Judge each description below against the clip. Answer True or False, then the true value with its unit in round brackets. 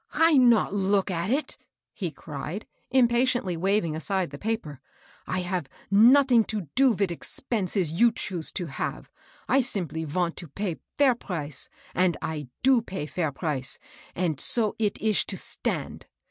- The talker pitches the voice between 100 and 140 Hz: False (190 Hz)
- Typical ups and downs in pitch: False (5.9 semitones)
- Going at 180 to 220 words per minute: False (165 wpm)